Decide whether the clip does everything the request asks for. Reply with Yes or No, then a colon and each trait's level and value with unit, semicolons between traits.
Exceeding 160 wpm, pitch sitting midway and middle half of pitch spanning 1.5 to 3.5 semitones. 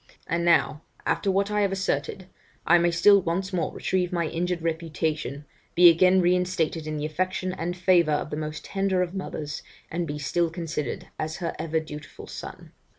Yes: average, 180 wpm; medium, 170 Hz; average, 2.8 semitones